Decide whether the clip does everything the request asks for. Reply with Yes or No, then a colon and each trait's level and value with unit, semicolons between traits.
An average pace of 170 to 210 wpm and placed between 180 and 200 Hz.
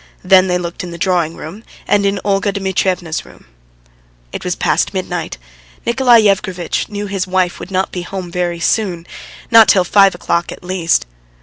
Yes: average, 175 wpm; medium, 185 Hz